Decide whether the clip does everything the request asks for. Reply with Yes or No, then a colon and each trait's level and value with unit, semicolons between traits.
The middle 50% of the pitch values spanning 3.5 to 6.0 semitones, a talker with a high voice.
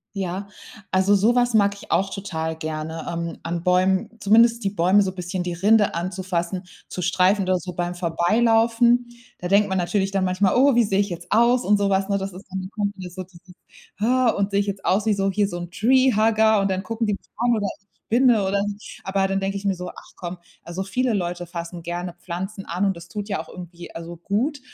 No: average, 2.8 semitones; high, 195 Hz